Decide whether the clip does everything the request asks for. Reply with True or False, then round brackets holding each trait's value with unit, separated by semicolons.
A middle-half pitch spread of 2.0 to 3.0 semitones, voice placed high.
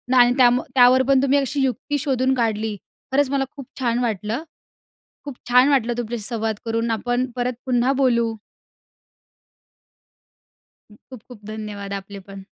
True (2.6 semitones; 245 Hz)